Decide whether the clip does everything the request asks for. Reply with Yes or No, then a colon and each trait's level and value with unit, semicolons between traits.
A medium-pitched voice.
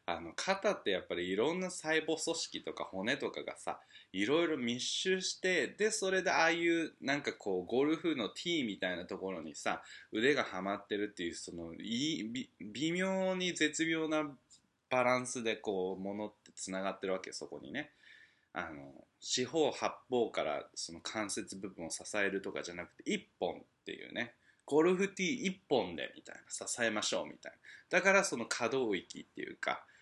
Yes: medium, 155 Hz